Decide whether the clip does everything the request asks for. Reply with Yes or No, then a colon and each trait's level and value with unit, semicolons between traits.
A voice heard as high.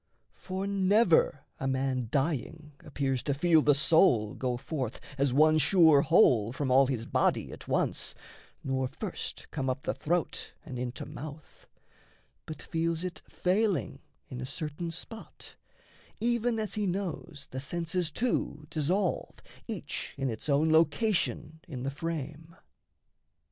No: medium, 155 Hz